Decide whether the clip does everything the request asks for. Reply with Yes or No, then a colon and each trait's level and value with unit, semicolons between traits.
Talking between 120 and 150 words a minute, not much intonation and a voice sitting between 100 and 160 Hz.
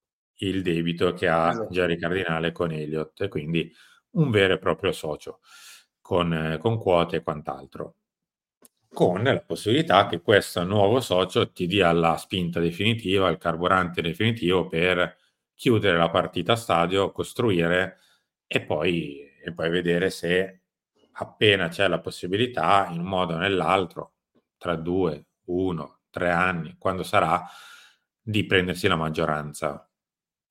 No: average, 135 wpm; narrow, 2.3 semitones; very low, 90 Hz